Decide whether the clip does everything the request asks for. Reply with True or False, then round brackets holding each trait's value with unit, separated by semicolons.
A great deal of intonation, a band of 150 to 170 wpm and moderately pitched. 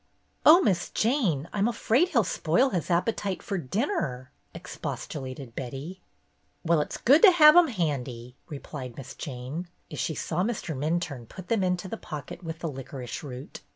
True (7.4 semitones; 160 wpm; 170 Hz)